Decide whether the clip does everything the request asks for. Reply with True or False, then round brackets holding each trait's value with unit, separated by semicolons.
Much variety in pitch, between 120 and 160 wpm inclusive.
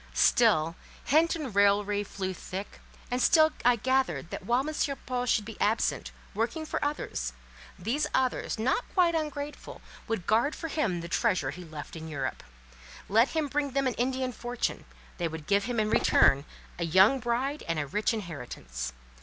False (6.9 semitones; 170 wpm)